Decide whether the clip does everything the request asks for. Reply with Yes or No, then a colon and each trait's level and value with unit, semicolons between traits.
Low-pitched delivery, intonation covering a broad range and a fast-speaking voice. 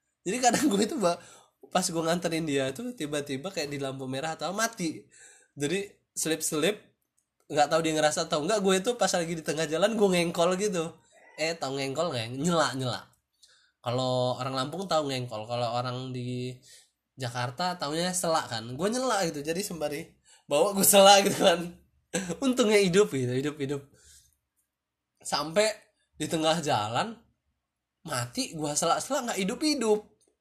No: medium, 160 Hz; wide, 6.4 semitones; fast, 155 wpm